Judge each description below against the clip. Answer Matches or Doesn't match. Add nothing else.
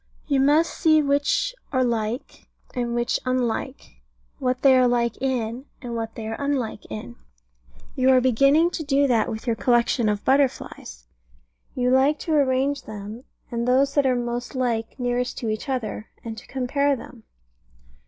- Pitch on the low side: Doesn't match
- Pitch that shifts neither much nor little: Matches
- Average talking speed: Matches